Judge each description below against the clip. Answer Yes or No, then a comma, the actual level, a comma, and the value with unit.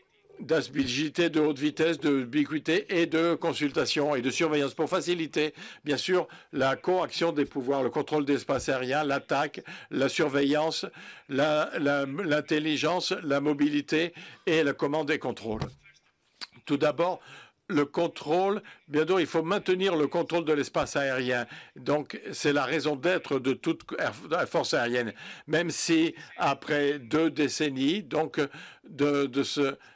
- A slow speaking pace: Yes, slow, 140 wpm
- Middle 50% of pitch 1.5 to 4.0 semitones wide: Yes, average, 2.8 semitones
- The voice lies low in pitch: No, medium, 150 Hz